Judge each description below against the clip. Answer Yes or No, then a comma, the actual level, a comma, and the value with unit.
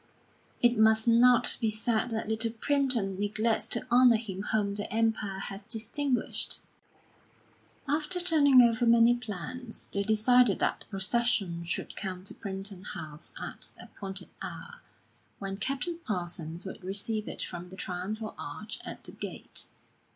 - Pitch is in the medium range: No, high, 220 Hz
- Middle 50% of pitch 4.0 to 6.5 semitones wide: No, average, 3.6 semitones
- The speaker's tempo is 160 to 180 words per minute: No, average, 145 wpm